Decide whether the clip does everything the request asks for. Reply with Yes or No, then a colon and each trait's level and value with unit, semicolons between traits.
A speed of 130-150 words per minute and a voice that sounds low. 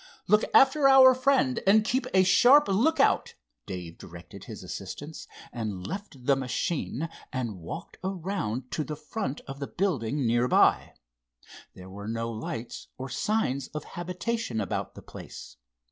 No: average, 145 wpm; medium, 145 Hz